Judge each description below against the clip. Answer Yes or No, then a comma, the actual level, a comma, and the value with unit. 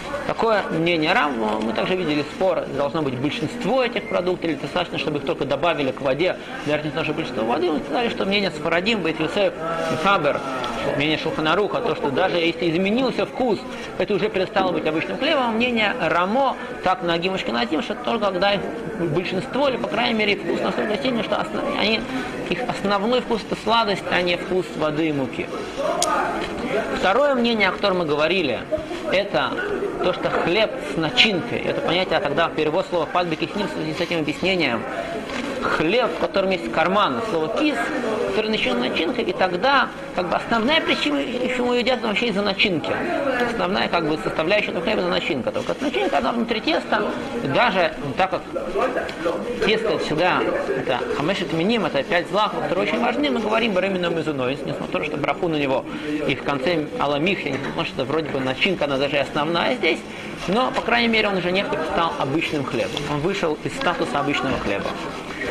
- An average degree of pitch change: No, wide, 6.2 semitones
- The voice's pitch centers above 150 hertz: Yes, medium, 185 Hz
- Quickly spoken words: Yes, fast, 180 wpm